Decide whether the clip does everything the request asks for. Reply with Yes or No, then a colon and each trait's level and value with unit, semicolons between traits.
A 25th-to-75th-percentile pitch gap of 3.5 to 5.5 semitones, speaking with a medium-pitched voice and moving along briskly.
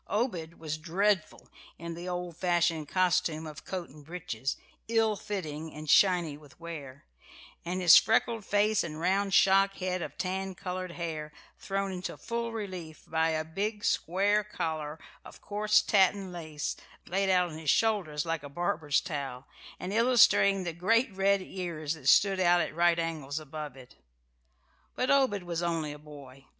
No: average, 3.9 semitones; medium, 175 Hz; average, 160 wpm